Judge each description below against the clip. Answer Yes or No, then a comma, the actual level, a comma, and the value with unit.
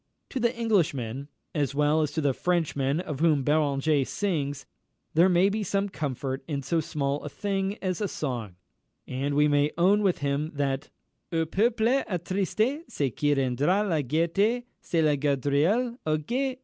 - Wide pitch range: Yes, wide, 5.7 semitones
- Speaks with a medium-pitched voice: Yes, medium, 155 Hz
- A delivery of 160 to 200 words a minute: Yes, average, 165 wpm